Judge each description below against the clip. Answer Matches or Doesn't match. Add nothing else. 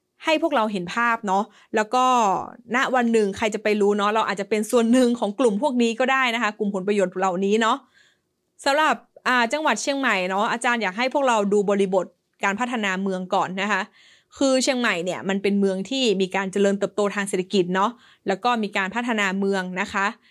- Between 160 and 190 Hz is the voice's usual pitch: Doesn't match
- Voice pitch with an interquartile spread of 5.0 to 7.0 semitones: Doesn't match